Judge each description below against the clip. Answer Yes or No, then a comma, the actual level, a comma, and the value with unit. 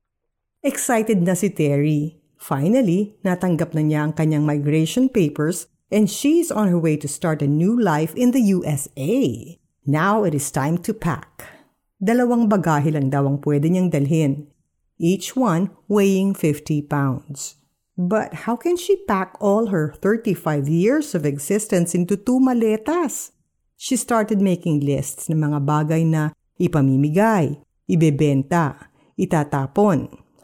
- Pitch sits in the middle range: Yes, medium, 170 Hz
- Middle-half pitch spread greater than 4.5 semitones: Yes, wide, 5.5 semitones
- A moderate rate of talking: Yes, average, 135 wpm